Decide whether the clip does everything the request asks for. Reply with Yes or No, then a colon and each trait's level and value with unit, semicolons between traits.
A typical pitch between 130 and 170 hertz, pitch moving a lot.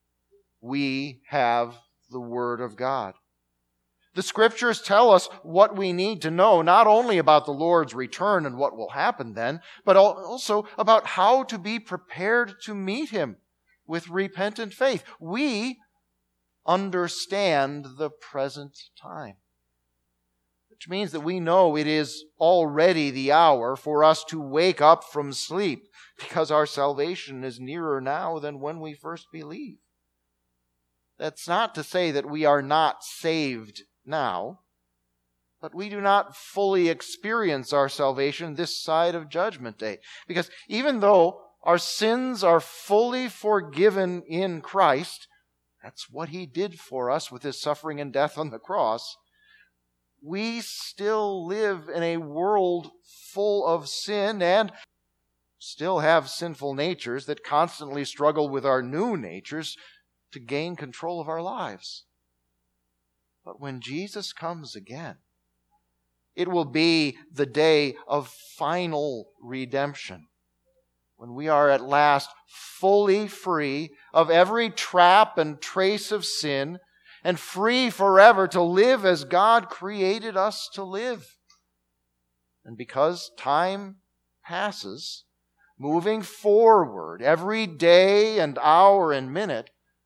Yes: medium, 160 Hz; wide, 6.5 semitones